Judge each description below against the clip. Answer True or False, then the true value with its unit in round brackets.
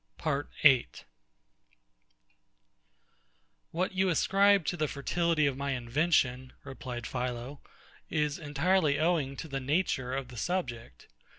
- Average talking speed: False (115 wpm)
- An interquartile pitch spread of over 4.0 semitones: True (4.7 semitones)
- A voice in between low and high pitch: True (145 Hz)